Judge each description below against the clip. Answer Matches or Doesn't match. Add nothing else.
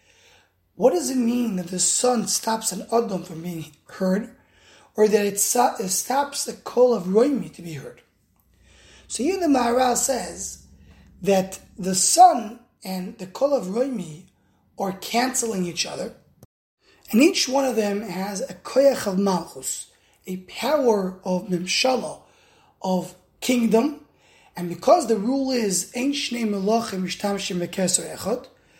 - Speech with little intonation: Doesn't match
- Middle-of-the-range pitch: Doesn't match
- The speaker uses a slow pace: Matches